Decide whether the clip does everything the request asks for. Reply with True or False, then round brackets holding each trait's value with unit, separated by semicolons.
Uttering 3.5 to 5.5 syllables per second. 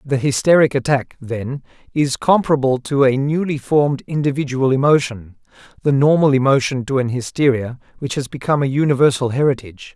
False (5.7 syllables/s)